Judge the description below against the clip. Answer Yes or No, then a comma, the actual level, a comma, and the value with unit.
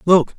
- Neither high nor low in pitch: Yes, medium, 175 Hz